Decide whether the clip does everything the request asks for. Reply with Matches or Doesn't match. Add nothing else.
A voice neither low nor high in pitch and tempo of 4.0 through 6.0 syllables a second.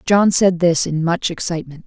Matches